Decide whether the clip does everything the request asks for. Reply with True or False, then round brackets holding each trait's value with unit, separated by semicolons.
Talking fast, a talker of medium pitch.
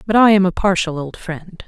True (250 wpm; 180 Hz)